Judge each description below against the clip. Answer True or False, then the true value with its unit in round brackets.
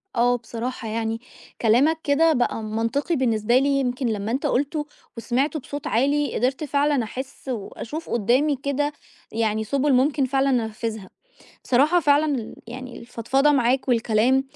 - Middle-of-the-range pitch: False (255 Hz)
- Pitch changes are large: False (3.7 semitones)